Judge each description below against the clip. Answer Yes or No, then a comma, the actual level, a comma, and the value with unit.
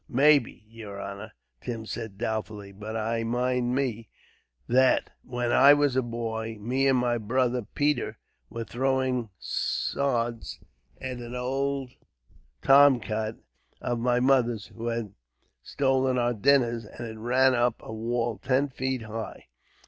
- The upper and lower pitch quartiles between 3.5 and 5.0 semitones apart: No, narrow, 2.6 semitones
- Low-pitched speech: Yes, low, 120 Hz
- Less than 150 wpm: Yes, slow, 135 wpm